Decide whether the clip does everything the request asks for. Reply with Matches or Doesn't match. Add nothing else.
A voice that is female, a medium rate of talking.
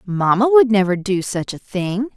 Matches